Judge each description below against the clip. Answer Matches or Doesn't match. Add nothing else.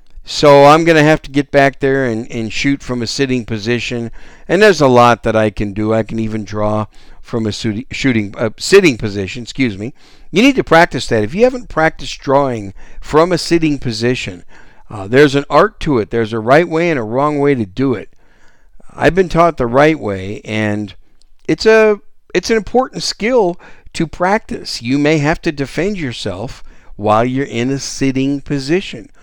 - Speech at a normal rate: Matches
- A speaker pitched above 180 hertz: Doesn't match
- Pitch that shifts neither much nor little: Doesn't match